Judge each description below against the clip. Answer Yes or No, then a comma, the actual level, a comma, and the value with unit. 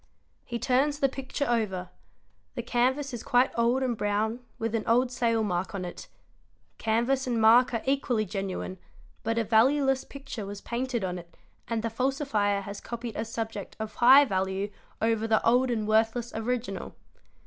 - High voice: Yes, high, 230 Hz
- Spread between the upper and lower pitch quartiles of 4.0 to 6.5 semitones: No, average, 2.9 semitones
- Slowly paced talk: No, average, 170 wpm